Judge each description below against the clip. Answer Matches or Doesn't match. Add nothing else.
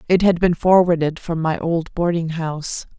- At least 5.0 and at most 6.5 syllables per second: Doesn't match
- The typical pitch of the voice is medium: Matches